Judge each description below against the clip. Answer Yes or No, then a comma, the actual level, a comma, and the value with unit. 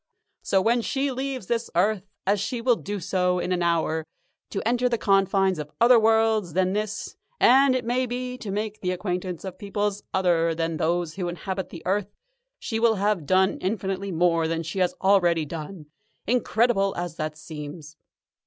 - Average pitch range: Yes, average, 4.3 semitones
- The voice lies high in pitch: Yes, high, 195 Hz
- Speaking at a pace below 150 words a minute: No, average, 180 wpm